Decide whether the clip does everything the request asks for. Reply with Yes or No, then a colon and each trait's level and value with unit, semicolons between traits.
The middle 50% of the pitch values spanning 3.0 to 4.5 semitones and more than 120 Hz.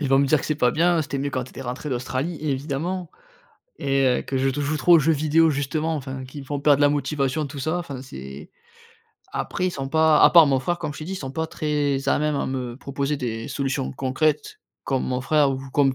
No: narrow, 2.5 semitones; medium, 140 Hz